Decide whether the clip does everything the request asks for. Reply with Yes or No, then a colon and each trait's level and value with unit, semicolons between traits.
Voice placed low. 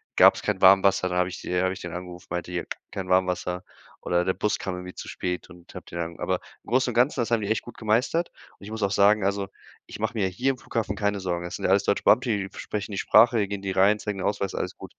Yes: low, 100 Hz